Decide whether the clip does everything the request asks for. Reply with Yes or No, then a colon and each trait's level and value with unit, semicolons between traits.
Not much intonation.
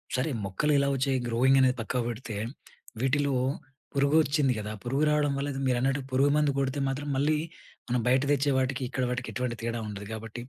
Yes: narrow, 2.3 semitones